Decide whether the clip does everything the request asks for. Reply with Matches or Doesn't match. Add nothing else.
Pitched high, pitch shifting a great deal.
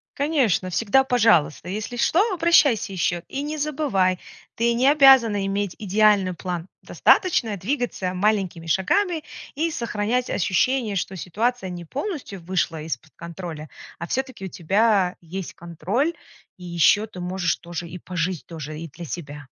Matches